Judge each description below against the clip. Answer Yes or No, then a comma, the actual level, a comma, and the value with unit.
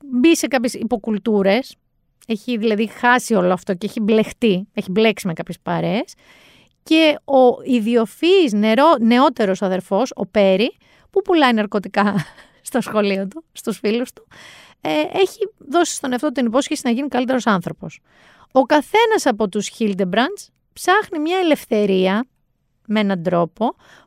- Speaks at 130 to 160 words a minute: Yes, average, 135 wpm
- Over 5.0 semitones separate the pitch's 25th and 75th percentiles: Yes, wide, 5.5 semitones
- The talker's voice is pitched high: Yes, high, 230 Hz